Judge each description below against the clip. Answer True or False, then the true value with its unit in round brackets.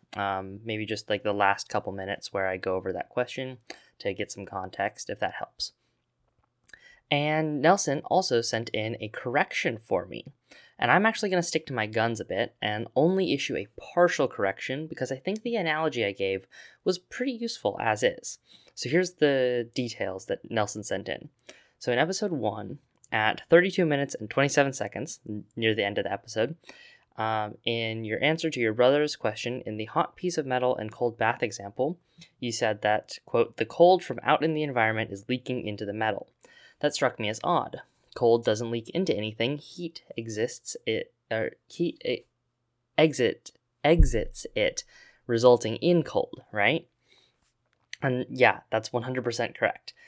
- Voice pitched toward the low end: True (125 Hz)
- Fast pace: False (175 wpm)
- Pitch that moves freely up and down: True (6.6 semitones)